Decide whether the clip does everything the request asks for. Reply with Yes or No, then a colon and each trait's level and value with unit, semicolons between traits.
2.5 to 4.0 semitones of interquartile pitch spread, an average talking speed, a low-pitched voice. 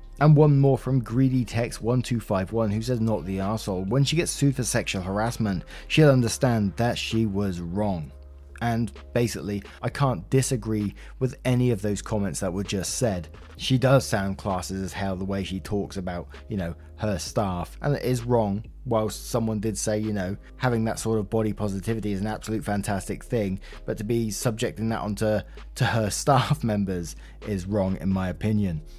Yes: average, 3.7 semitones; average, 185 wpm; low, 110 Hz